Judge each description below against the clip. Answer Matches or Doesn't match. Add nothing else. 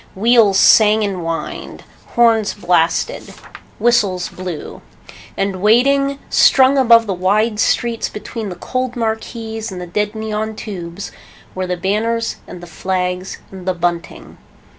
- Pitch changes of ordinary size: Matches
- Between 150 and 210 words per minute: Doesn't match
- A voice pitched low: Doesn't match